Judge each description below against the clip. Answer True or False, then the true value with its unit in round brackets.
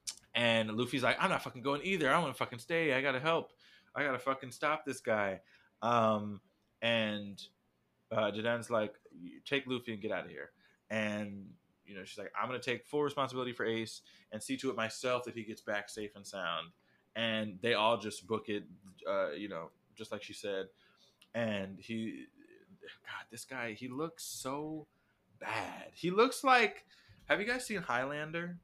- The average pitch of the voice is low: True (120 Hz)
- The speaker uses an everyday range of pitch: True (4.8 semitones)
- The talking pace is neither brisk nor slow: True (185 wpm)